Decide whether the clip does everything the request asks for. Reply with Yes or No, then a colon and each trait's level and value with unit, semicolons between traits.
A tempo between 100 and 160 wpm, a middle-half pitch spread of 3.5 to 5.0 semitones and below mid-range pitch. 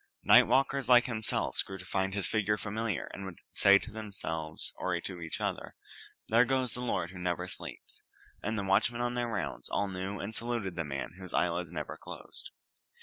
No: average, 195 wpm; average, 4.3 semitones; low, 100 Hz